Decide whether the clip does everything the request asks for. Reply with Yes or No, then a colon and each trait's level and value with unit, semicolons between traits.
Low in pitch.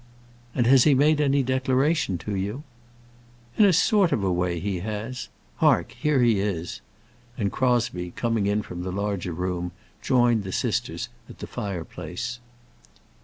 Yes: low, 105 Hz